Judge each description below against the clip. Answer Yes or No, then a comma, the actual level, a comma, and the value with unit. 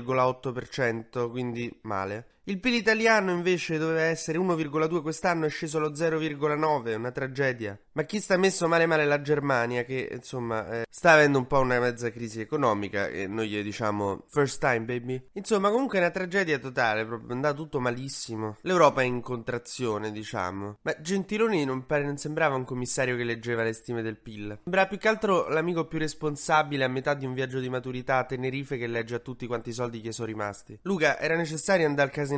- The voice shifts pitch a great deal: No, average, 5.0 semitones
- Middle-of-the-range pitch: No, low, 130 Hz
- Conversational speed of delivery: No, fast, 190 wpm